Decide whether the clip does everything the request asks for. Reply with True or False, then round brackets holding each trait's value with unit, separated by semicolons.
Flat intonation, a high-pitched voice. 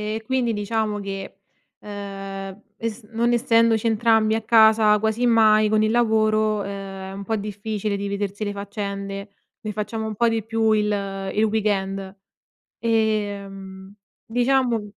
True (1.9 semitones; 215 Hz)